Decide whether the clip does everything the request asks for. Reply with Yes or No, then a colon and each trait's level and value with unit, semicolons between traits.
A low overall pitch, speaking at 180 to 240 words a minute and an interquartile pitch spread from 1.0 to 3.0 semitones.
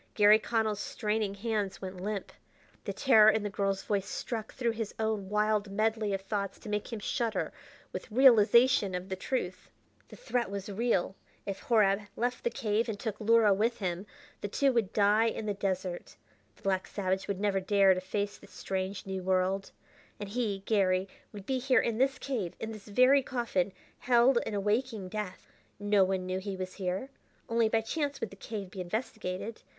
No: high, 210 Hz; average, 190 wpm; average, 2.7 semitones